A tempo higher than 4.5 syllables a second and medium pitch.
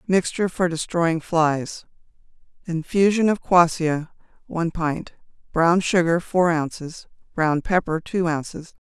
No: 4.1 syllables/s; medium, 170 Hz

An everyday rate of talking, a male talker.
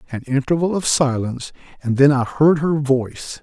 Yes: average, 175 wpm; male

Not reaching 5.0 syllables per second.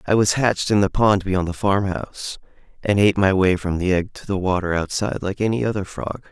No: 6.0 syllables/s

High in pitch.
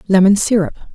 Yes: high, 195 Hz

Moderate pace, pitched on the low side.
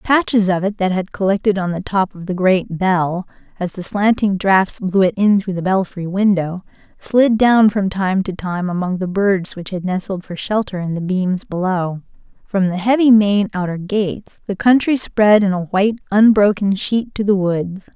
No: average, 195 wpm; high, 195 Hz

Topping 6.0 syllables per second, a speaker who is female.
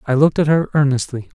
No: 6.9 syllables/s; male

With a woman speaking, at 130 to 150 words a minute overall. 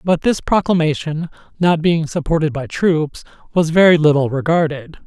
No: male; average, 140 wpm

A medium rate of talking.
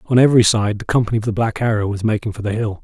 No: fast, 295 wpm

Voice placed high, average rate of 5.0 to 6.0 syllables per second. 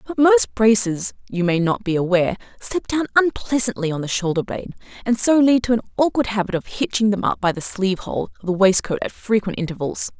Yes: high, 210 Hz; 5.8 syllables/s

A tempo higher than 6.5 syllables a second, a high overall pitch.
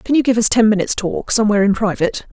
Yes: 7.5 syllables/s; high, 215 Hz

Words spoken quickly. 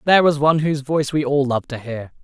Yes: fast, 270 wpm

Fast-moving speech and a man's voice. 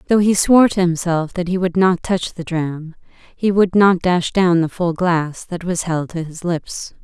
No: fast, 220 wpm; female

